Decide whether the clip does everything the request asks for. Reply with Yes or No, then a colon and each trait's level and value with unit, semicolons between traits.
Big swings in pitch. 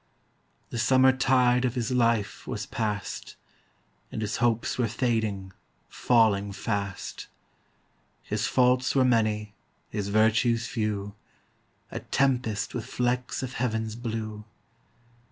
No: average, 2.8 semitones